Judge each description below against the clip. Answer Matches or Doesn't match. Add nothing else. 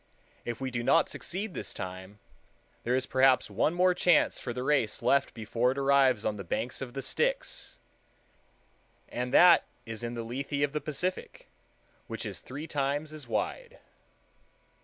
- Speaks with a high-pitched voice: Doesn't match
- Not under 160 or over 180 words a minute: Matches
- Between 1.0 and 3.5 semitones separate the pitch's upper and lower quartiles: Doesn't match